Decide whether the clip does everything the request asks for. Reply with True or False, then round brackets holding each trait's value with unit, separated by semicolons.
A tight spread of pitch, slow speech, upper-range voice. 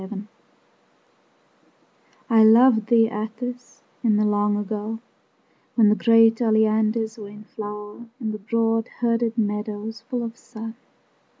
True (1.5 semitones; 125 wpm; 220 Hz)